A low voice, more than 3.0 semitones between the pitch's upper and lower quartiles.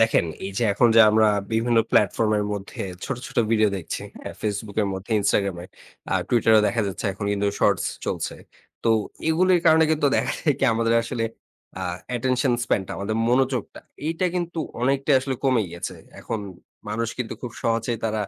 Yes: low, 115 Hz; average, 3.8 semitones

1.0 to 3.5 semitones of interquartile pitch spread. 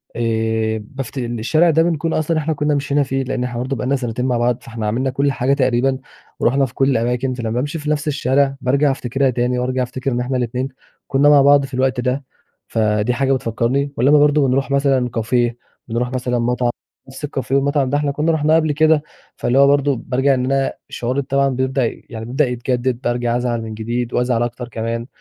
Yes: narrow, 2.5 semitones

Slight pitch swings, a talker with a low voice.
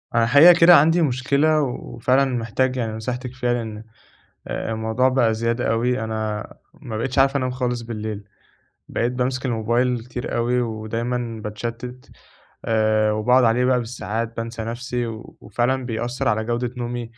Yes: narrow, 2.1 semitones; low, 120 Hz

